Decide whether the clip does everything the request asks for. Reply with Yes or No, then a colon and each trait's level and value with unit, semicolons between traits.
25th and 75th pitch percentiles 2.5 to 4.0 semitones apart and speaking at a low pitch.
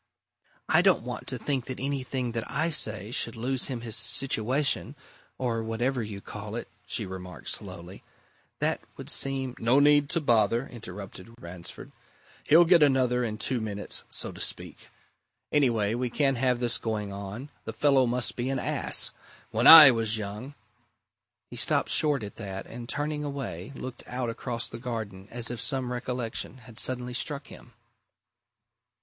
Yes: average, 3.5 semitones; low, 120 Hz